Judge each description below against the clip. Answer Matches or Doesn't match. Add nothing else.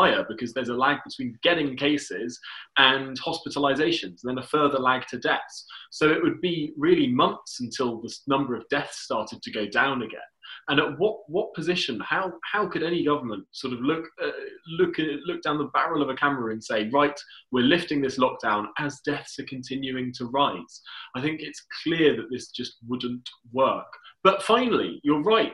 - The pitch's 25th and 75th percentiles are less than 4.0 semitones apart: Doesn't match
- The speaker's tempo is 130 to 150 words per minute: Doesn't match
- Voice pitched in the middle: Matches